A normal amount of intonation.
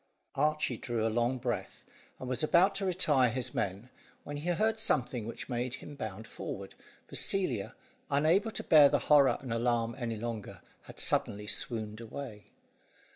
Yes: average, 4.9 semitones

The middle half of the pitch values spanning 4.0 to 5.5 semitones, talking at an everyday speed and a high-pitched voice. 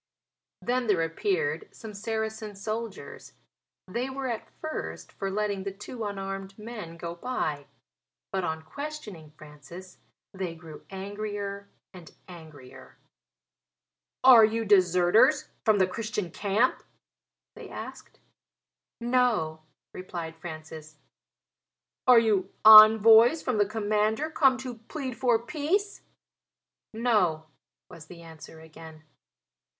No: average, 5.1 semitones; slow, 110 wpm; high, 205 Hz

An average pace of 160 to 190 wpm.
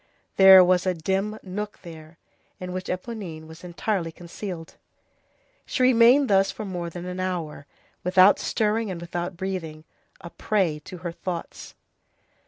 No: average, 145 wpm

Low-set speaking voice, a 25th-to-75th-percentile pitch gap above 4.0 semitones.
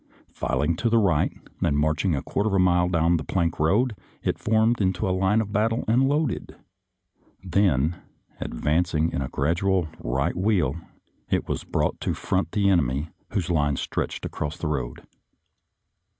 Yes: very low, 90 Hz; average, 5.0 semitones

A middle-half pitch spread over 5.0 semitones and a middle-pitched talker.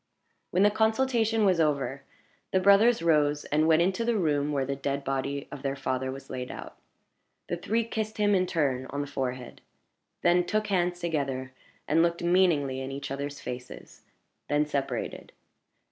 Yes: wide, 5.4 semitones; medium, 150 Hz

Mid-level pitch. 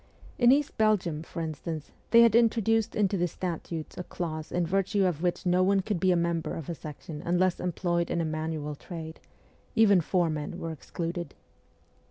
Yes: medium, 175 Hz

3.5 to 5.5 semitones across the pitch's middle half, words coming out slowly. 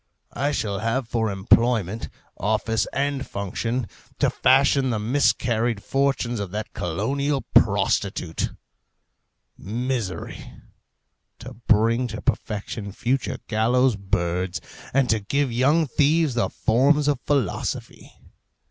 Yes: average, 4.3 semitones; slow, 110 wpm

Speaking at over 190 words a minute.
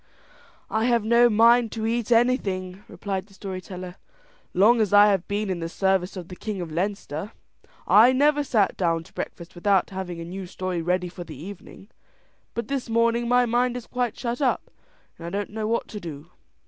Yes: average, 200 wpm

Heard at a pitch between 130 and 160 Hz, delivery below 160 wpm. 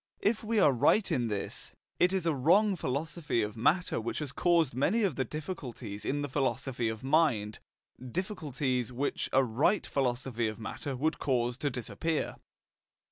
No: low, 135 Hz; average, 165 wpm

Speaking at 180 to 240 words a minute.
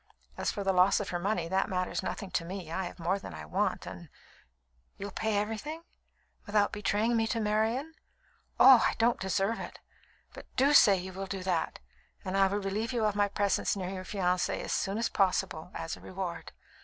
Yes: fast, 205 wpm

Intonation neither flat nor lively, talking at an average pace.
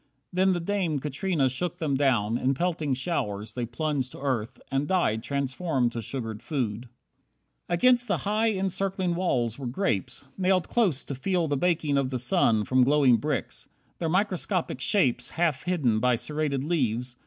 No: wide, 6.2 semitones; average, 165 wpm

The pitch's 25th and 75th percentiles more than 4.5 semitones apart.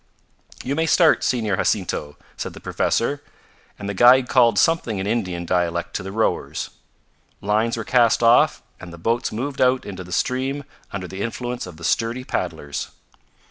Yes: wide, 5.4 semitones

